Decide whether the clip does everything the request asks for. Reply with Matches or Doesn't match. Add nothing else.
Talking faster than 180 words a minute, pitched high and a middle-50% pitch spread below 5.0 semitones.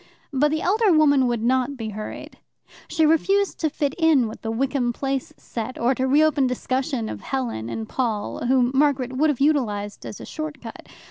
Matches